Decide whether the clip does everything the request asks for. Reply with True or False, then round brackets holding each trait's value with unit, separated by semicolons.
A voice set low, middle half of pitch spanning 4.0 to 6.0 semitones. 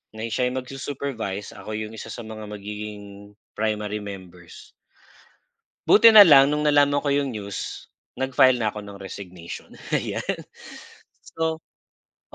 True (110 Hz; 5.1 semitones)